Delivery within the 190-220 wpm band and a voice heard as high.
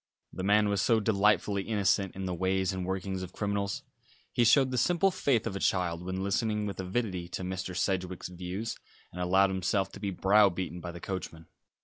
No: average, 195 wpm; very low, 95 Hz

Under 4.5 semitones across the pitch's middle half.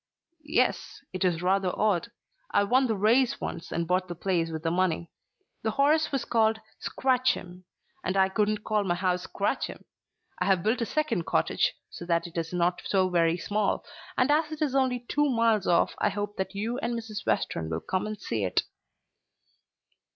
No: average, 4.8 semitones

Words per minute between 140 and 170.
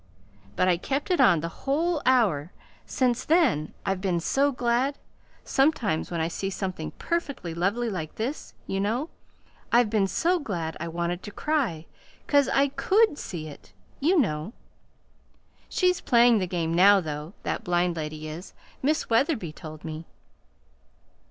Yes: average, 150 wpm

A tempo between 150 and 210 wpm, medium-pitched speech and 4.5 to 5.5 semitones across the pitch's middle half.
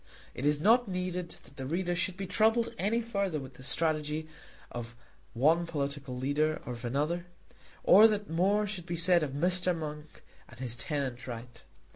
Yes: average, 175 wpm; medium, 160 Hz; average, 4.8 semitones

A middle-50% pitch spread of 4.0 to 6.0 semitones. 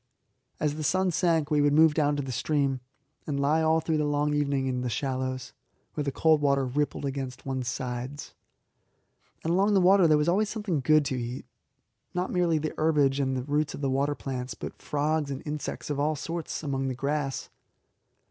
No: narrow, 2.6 semitones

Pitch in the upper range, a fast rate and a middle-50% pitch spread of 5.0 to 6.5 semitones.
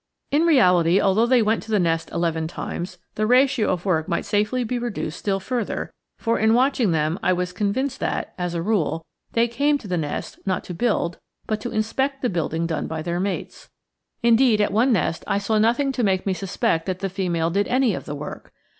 Yes: high, 200 Hz; fast, 215 wpm; average, 5.3 semitones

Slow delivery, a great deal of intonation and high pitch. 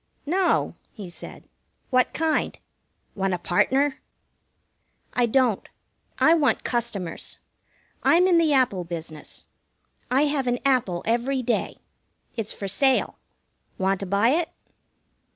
Yes: slow, 120 wpm; wide, 6.4 semitones; high, 245 Hz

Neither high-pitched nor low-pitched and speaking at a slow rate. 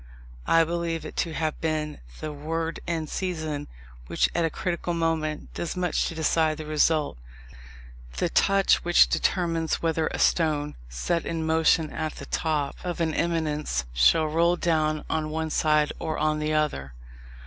No: medium, 160 Hz; average, 160 wpm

